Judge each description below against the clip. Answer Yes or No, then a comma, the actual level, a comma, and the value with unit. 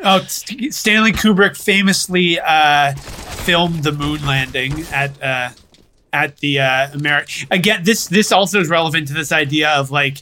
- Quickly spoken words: No, average, 155 wpm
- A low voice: No, medium, 155 Hz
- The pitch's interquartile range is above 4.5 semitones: Yes, average, 5.2 semitones